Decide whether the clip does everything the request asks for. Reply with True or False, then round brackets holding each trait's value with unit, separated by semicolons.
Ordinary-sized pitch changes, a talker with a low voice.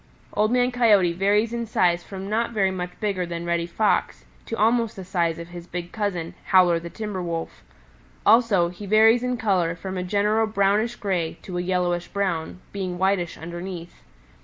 False (3.6 semitones; 190 Hz)